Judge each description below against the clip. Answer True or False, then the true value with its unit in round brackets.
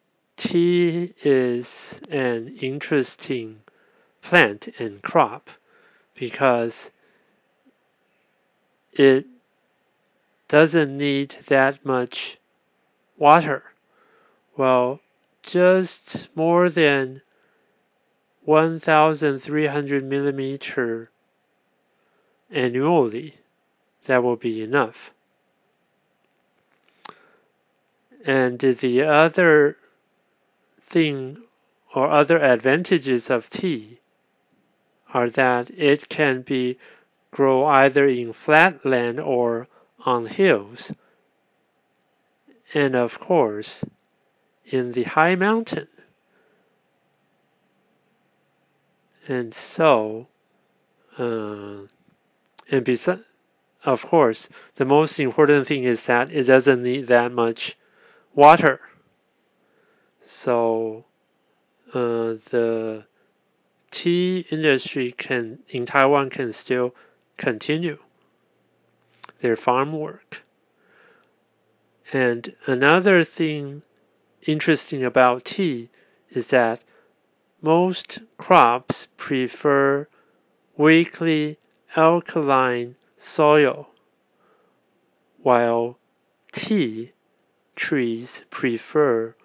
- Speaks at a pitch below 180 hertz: True (135 Hz)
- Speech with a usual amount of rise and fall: True (4.0 semitones)